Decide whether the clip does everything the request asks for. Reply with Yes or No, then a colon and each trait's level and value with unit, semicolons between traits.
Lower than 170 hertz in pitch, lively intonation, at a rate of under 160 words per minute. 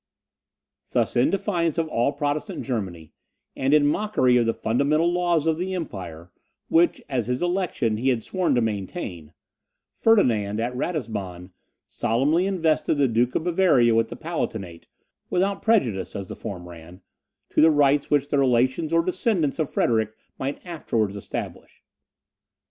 Yes: low, 135 Hz; wide, 7.1 semitones; average, 150 wpm